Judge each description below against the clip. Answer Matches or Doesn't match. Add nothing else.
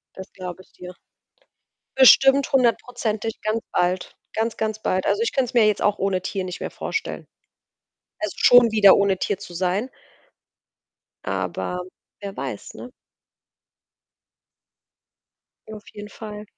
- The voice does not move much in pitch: Doesn't match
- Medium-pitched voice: Doesn't match